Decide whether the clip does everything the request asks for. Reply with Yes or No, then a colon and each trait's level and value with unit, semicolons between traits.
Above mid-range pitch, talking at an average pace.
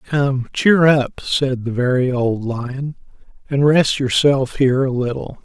No: low, 135 Hz; average, 155 wpm